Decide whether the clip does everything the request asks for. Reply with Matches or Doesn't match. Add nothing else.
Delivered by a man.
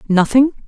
Doesn't match